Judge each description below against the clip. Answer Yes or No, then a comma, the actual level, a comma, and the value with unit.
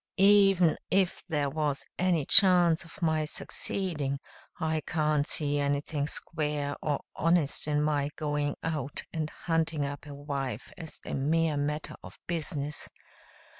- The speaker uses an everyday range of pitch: No, narrow, 2.2 semitones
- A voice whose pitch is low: No, medium, 150 Hz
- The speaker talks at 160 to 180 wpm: No, slow, 135 wpm